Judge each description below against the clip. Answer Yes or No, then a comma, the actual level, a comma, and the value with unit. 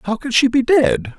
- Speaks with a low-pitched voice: No, high, 190 Hz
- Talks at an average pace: No, fast, 255 wpm